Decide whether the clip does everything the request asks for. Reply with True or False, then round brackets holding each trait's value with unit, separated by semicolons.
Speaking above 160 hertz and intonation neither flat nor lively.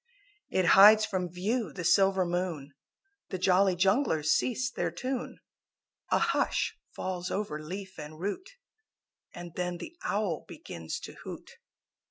True (185 Hz; 3.0 semitones)